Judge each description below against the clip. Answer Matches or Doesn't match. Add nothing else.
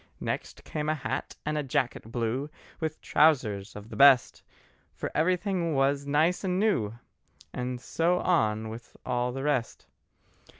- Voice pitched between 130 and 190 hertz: Matches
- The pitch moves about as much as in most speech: Matches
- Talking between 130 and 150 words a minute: Matches